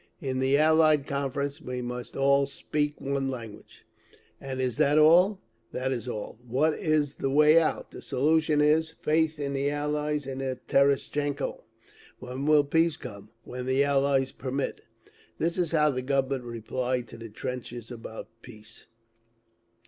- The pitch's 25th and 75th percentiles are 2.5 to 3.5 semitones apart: Yes, average, 2.9 semitones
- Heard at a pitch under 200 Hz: Yes, medium, 140 Hz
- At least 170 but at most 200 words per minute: No, average, 155 wpm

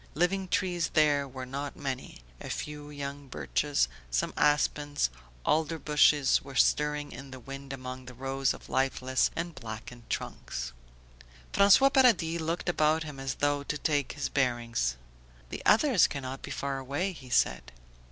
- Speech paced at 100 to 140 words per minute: No, average, 150 wpm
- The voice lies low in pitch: No, medium, 145 Hz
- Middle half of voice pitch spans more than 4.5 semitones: No, average, 3.0 semitones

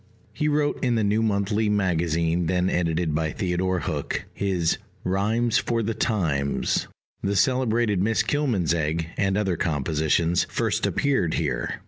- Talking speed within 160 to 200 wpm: No, slow, 135 wpm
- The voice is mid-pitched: No, very low, 95 Hz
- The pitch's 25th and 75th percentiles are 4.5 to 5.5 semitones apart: Yes, average, 5.0 semitones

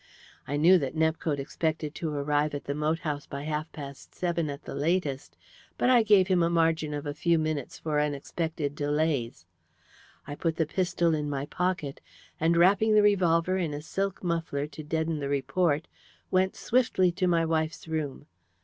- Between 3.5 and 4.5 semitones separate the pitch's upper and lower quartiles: No, average, 2.8 semitones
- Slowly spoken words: No, average, 180 wpm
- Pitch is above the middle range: No, medium, 160 Hz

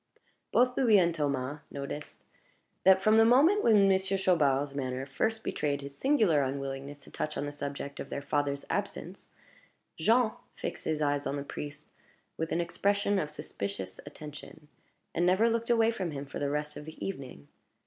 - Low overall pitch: No, medium, 150 Hz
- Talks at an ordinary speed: Yes, average, 175 wpm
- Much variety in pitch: Yes, wide, 5.8 semitones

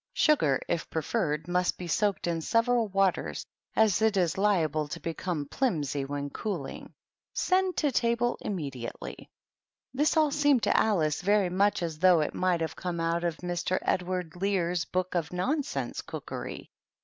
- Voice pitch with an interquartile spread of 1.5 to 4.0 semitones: No, average, 4.7 semitones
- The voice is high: No, medium, 180 Hz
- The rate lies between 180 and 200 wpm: No, average, 155 wpm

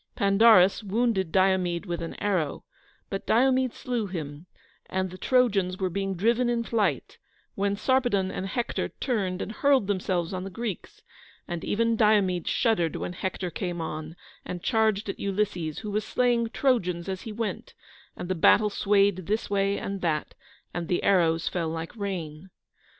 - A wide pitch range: No, average, 3.7 semitones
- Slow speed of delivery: No, average, 160 wpm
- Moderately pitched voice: No, high, 195 Hz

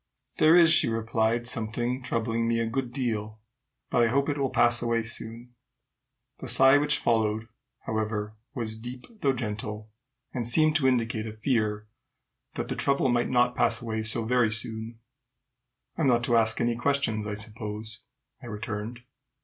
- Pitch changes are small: Yes, narrow, 2.1 semitones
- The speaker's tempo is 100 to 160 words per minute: No, average, 170 wpm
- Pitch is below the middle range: Yes, low, 115 Hz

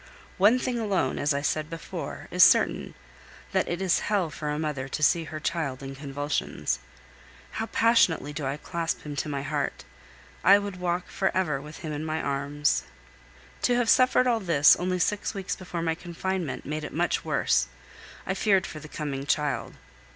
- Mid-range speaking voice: Yes, medium, 160 Hz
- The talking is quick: No, average, 185 wpm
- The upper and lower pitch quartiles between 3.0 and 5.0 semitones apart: Yes, average, 4.3 semitones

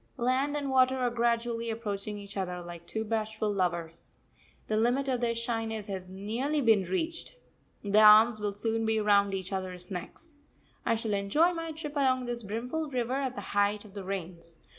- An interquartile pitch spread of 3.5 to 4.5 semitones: Yes, average, 4.0 semitones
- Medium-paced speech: Yes, average, 185 wpm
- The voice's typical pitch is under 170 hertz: No, high, 220 Hz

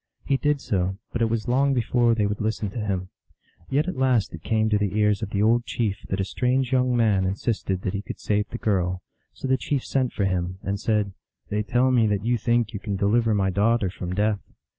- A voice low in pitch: Yes, low, 105 Hz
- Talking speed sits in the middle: No, fast, 235 wpm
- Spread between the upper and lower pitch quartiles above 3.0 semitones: Yes, average, 3.4 semitones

